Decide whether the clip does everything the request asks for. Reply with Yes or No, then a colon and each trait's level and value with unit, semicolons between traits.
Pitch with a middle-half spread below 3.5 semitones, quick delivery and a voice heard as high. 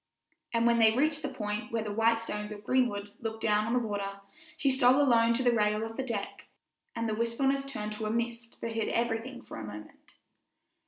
Yes: narrow, 2.5 semitones; fast, 215 wpm; high, 230 Hz